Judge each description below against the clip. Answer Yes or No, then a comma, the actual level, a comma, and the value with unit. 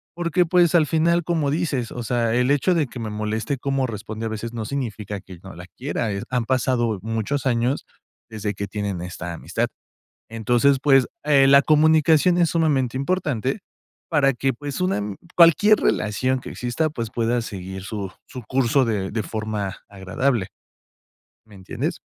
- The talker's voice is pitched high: No, low, 120 Hz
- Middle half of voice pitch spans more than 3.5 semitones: Yes, average, 5.2 semitones